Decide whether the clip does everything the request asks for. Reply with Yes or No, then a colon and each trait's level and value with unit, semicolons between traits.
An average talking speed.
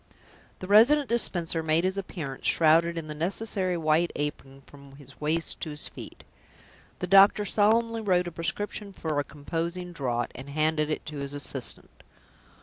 Yes: average, 160 wpm